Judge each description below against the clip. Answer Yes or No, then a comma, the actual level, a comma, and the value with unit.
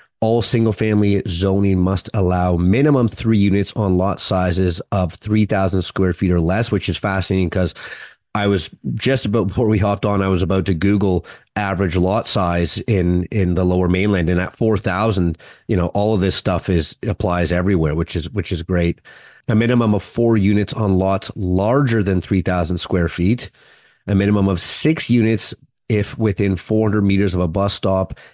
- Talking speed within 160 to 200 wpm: Yes, average, 180 wpm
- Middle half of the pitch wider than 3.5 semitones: No, average, 2.9 semitones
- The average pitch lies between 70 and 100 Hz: Yes, very low, 95 Hz